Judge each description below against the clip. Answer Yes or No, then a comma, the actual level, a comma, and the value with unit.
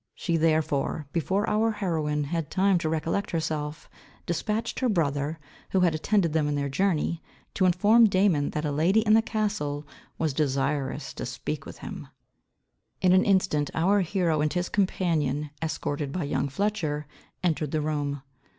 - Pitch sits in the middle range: Yes, medium, 160 Hz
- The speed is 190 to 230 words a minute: No, average, 160 wpm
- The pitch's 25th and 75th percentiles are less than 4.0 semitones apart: No, average, 4.3 semitones